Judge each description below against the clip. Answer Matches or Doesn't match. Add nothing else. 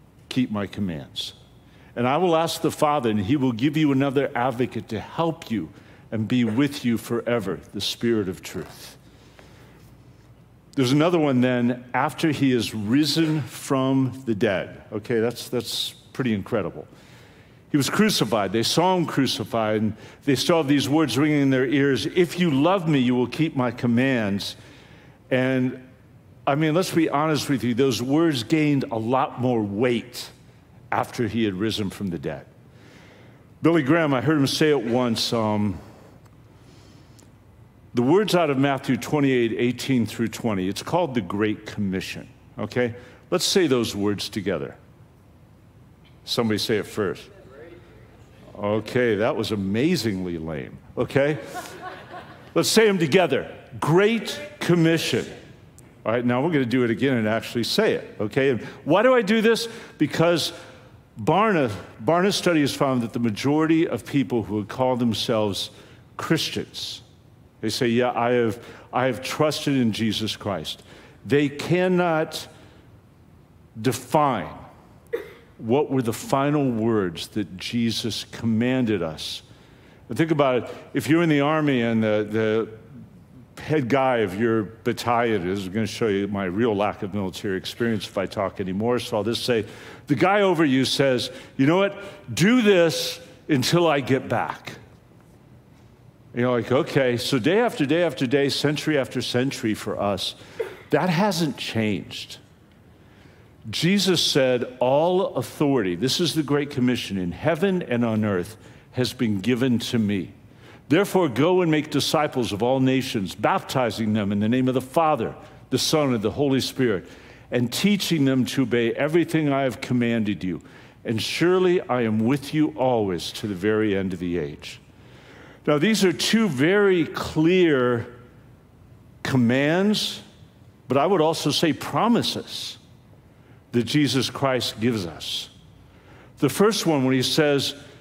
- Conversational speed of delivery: Matches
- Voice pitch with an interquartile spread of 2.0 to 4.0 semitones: Doesn't match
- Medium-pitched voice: Doesn't match